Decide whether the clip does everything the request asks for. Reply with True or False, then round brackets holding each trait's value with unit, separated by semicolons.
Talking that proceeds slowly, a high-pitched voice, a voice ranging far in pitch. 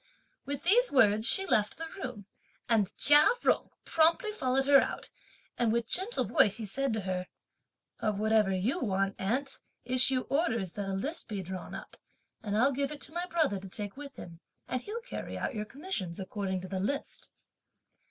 False (185 wpm; 235 Hz; 6.2 semitones)